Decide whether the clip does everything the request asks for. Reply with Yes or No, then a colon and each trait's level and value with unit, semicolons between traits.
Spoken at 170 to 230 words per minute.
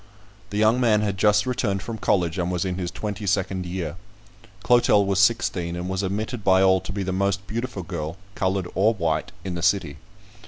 Yes: average, 200 wpm